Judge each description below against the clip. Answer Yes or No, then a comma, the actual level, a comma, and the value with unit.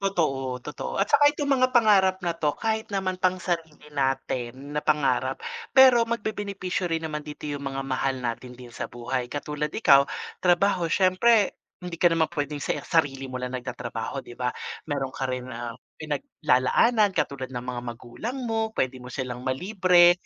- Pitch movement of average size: No, wide, 6.5 semitones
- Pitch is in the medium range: Yes, medium, 150 Hz